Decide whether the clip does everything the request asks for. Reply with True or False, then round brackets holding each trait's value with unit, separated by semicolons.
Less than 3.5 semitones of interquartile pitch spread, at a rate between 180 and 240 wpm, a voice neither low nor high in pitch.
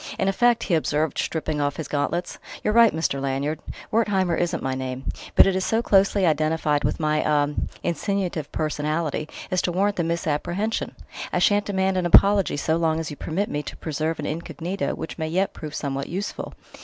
False (4.2 semitones; 190 wpm; 165 Hz)